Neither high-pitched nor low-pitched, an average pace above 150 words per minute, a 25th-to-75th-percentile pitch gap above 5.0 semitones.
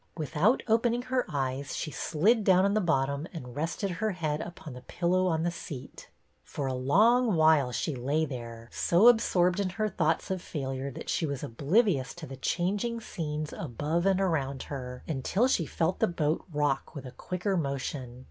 Yes: medium, 160 Hz; average, 185 wpm; wide, 5.4 semitones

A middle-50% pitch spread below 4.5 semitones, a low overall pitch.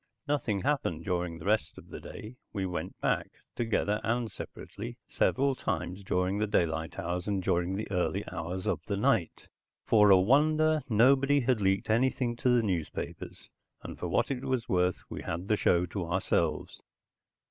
No: wide, 5.5 semitones; low, 105 Hz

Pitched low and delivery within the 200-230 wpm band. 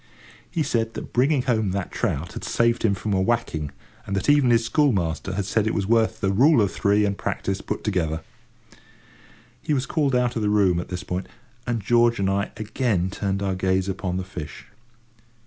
Yes: low, 105 Hz; fast, 205 wpm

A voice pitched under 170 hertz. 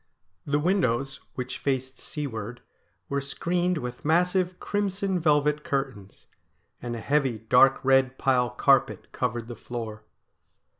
Yes: low, 135 Hz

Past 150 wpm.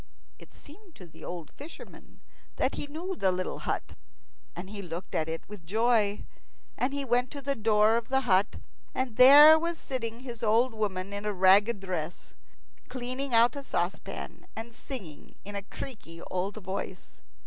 Yes: average, 170 wpm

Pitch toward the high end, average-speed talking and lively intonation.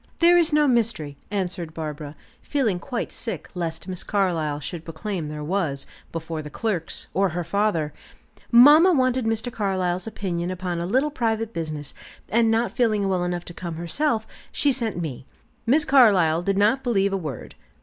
Yes: high, 195 Hz; average, 170 wpm; wide, 5.8 semitones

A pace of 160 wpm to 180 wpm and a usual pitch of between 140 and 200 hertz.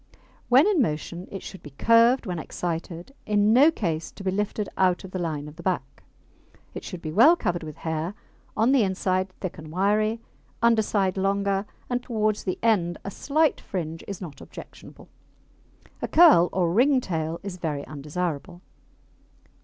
Yes: average, 170 wpm; high, 190 Hz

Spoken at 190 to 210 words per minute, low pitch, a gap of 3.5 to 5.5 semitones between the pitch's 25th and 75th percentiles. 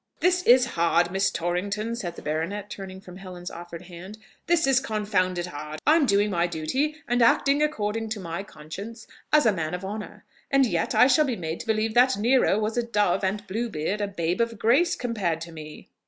No: average, 200 wpm; high, 205 Hz; average, 5.2 semitones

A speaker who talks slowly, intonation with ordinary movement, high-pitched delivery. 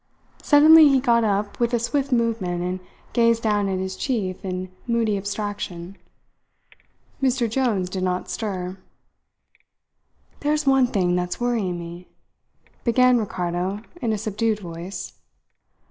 Yes: slow, 130 wpm; average, 4.5 semitones; high, 210 Hz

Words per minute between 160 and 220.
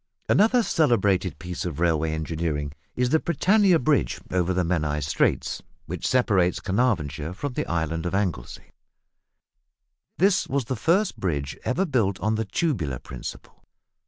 No: average, 140 wpm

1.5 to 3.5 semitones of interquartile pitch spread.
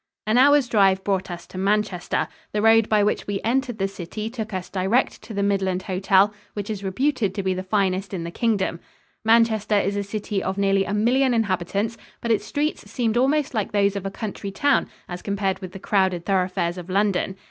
Yes: average, 2.8 semitones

